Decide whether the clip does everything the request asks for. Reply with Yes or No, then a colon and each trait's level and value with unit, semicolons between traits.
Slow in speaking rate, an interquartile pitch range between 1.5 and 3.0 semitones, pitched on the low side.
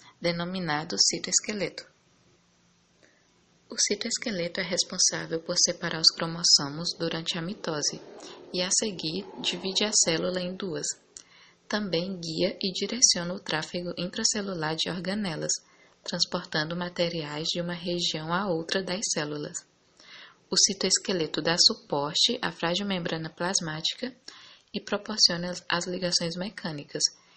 No: slow, 115 wpm; narrow, 2.5 semitones; medium, 175 Hz